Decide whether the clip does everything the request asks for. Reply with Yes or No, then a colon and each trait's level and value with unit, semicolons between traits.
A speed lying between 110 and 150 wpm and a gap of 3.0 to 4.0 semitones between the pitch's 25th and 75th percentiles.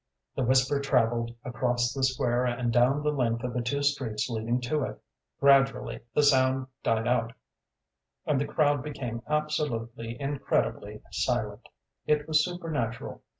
Yes: average, 145 wpm; average, 3.3 semitones